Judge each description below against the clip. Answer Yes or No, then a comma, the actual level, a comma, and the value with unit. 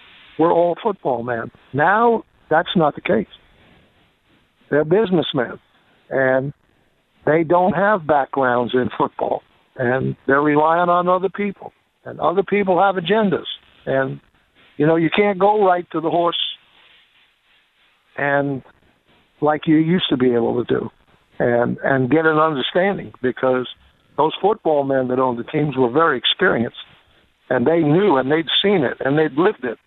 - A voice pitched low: No, medium, 155 Hz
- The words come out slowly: No, average, 150 wpm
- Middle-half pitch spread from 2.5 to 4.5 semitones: No, average, 5.3 semitones